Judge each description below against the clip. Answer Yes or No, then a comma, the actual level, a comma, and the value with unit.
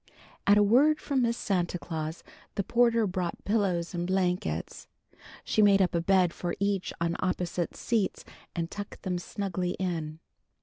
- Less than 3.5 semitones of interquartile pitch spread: Yes, average, 2.9 semitones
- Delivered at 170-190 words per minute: No, average, 160 wpm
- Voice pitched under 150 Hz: No, medium, 185 Hz